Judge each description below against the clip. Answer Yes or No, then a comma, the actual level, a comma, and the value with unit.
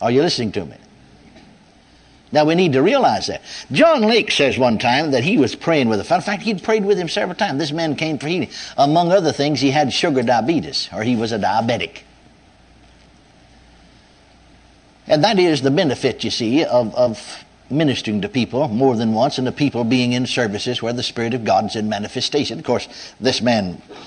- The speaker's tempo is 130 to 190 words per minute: No, average, 200 wpm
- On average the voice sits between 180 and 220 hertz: No, low, 135 Hz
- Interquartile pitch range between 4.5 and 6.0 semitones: Yes, wide, 5.6 semitones